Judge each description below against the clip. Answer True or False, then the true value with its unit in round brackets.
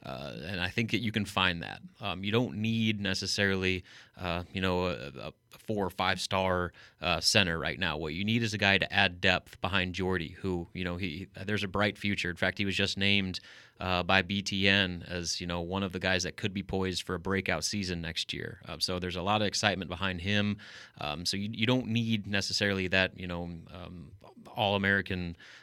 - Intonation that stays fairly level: True (2.1 semitones)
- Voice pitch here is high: False (95 Hz)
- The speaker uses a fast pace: True (220 wpm)